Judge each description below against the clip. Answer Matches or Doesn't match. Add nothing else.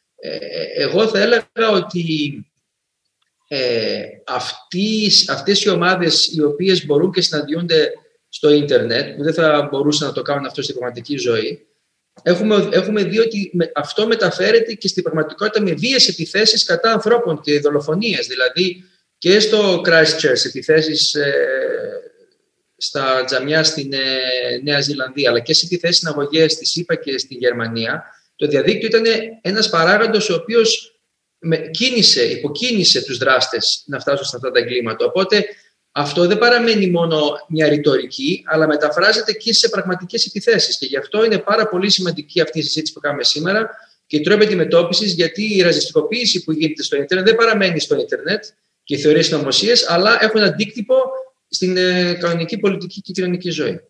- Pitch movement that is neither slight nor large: Doesn't match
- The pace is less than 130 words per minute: Doesn't match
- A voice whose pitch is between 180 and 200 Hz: Matches